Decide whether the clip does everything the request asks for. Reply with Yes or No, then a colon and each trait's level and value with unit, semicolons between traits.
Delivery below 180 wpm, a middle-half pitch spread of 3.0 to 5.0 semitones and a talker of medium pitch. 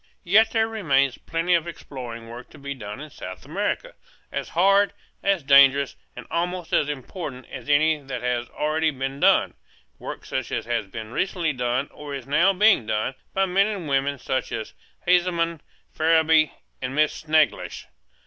Yes: average, 170 wpm; average, 4.6 semitones; medium, 150 Hz